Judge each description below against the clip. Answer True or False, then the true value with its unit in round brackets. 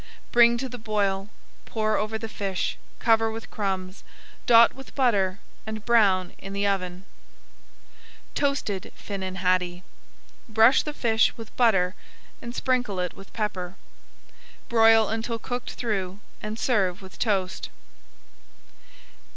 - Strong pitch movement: False (3.3 semitones)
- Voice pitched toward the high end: True (215 Hz)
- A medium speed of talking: False (125 wpm)